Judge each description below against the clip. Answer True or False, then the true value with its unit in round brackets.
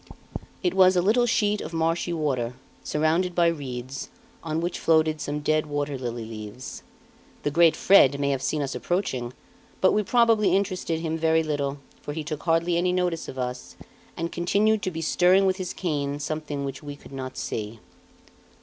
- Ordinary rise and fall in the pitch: True (4.2 semitones)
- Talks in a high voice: False (160 Hz)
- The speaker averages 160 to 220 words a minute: True (180 wpm)